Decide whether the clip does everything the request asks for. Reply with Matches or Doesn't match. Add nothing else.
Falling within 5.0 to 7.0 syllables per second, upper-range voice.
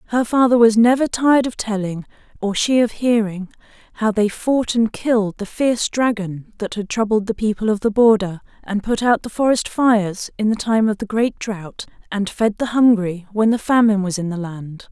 Matches